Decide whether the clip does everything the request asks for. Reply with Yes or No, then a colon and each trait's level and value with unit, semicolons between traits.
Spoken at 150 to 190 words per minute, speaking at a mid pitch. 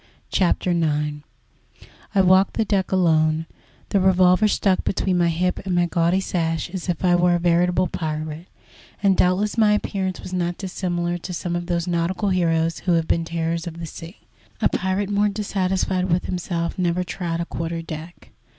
Yes: average, 180 wpm; medium, 175 Hz